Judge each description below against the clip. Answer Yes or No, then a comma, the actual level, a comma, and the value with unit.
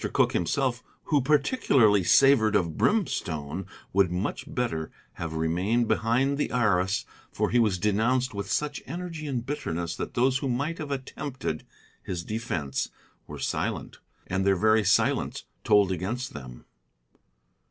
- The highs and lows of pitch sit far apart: Yes, wide, 6.5 semitones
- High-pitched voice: No, low, 110 Hz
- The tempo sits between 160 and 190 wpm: No, average, 140 wpm